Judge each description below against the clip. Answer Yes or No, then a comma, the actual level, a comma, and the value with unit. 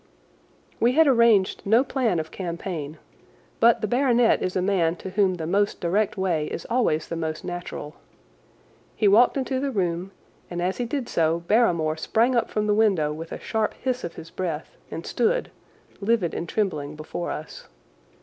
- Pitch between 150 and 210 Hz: Yes, high, 190 Hz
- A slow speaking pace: No, average, 180 wpm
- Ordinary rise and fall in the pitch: No, wide, 5.7 semitones